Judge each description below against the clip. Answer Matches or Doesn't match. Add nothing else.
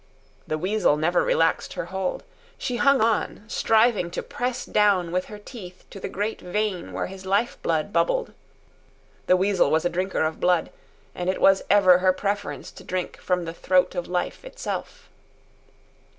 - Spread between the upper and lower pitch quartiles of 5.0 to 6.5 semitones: Doesn't match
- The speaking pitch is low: Doesn't match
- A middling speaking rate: Matches